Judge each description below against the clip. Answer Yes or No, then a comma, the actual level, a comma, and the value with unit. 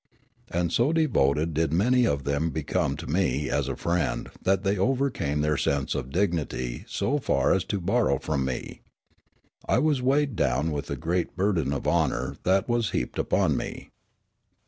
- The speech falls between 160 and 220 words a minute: Yes, average, 170 wpm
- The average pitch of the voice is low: Yes, very low, 85 Hz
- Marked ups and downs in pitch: Yes, wide, 7.1 semitones